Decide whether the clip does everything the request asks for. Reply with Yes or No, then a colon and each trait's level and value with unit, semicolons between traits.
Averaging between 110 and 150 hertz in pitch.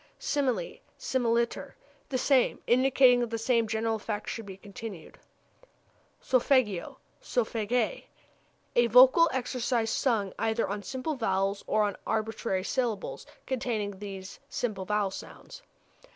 No: high, 230 Hz